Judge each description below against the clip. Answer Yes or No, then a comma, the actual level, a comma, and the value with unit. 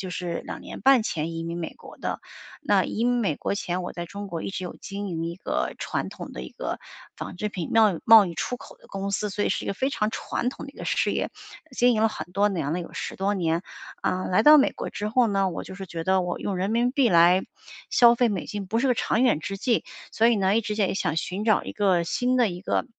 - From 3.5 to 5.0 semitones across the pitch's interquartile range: Yes, average, 4.0 semitones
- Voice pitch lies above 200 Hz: No, high, 195 Hz